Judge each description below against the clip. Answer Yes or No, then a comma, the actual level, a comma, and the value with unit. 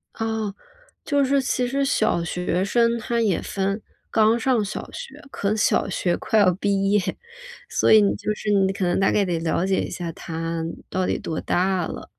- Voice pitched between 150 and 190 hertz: No, high, 200 Hz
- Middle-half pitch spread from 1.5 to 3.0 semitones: No, average, 3.5 semitones